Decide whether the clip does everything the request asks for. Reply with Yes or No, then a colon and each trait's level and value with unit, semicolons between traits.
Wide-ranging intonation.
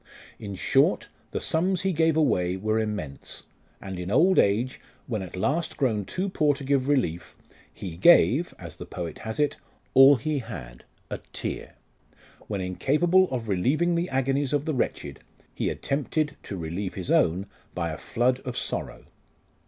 Yes: wide, 8.1 semitones